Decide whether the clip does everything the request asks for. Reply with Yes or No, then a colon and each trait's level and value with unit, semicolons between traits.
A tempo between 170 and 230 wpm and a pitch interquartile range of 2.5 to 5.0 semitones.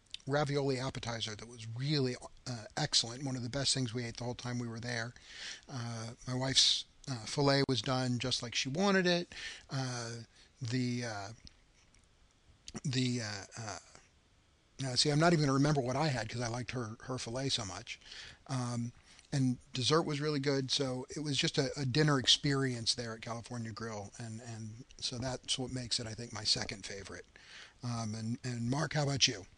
Yes: average, 190 wpm; average, 3.0 semitones